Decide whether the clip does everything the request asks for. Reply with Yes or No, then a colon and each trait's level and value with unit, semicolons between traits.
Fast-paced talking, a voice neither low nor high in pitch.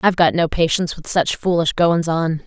Yes: fast, 220 wpm; medium, 165 Hz